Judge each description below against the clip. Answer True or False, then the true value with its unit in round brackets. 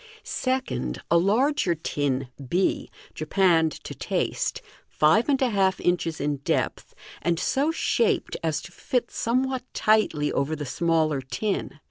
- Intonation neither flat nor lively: False (7.2 semitones)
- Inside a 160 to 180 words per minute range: False (135 wpm)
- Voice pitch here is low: False (175 Hz)